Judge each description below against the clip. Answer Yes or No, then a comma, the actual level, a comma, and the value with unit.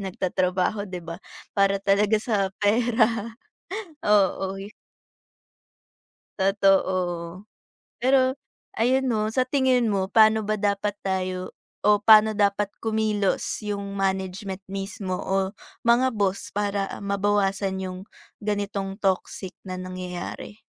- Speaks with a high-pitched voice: Yes, high, 200 Hz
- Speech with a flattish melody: Yes, narrow, 2.1 semitones